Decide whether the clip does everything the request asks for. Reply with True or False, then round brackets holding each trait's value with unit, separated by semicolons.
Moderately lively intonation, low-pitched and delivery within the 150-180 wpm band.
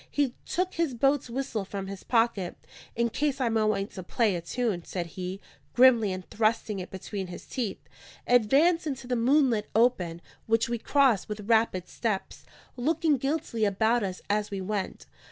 False (4.6 semitones; 225 Hz; 170 wpm)